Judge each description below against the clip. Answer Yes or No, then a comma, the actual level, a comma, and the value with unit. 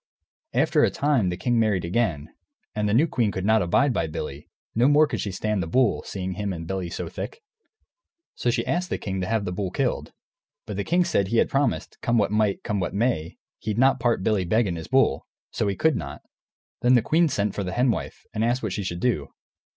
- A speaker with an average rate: No, fast, 235 wpm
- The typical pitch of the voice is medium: No, low, 105 Hz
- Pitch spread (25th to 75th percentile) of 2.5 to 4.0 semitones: No, average, 4.7 semitones